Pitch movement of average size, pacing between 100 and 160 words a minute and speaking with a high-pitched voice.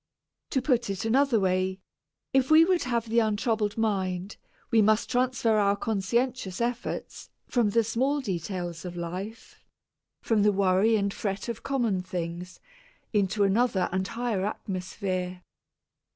Yes: average, 3.9 semitones; average, 140 wpm; high, 210 Hz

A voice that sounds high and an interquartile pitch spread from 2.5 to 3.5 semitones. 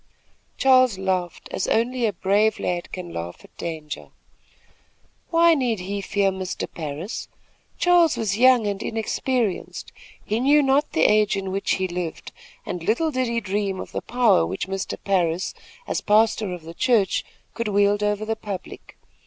No: high, 205 Hz; average, 4.0 semitones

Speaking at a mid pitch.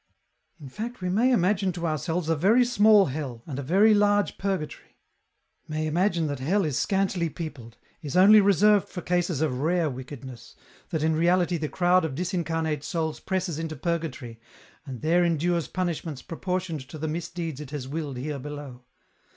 Yes: medium, 165 Hz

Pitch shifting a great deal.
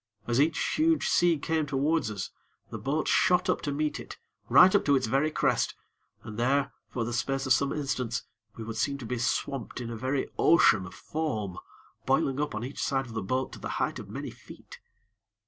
No: average, 4.2 semitones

